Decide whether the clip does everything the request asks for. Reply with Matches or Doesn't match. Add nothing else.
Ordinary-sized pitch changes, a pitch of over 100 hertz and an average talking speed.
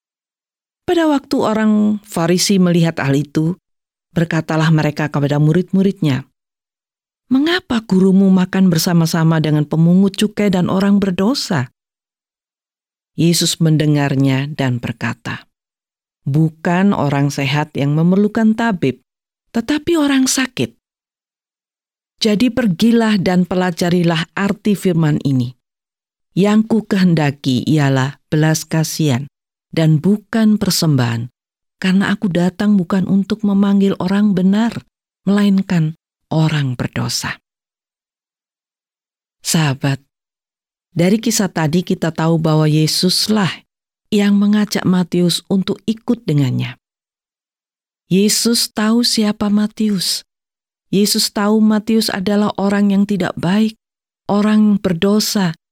Matches